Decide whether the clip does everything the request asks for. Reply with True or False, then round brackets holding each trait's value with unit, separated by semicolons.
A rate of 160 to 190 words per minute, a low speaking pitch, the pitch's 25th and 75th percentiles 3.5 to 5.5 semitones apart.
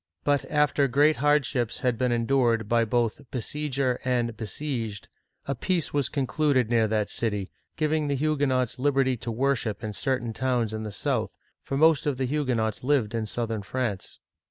True (170 wpm; 125 Hz; 3.9 semitones)